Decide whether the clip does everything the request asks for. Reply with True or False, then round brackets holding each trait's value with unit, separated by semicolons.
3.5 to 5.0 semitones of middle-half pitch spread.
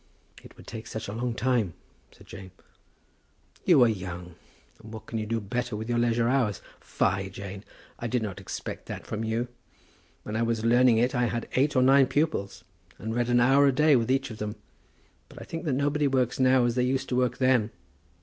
False (2.9 semitones)